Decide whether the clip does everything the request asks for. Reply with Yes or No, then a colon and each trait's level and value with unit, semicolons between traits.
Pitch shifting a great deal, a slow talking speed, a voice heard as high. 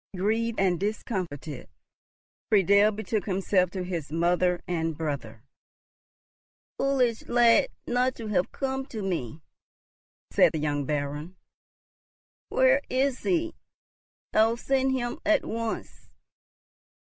Yes: wide, 6.3 semitones; slow, 110 wpm; high, 200 Hz